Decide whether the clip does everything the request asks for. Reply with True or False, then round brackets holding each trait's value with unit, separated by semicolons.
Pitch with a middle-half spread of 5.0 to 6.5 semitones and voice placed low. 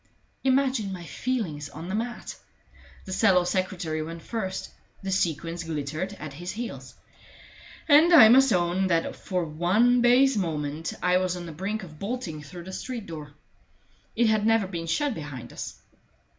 False (5.4 semitones; 185 Hz)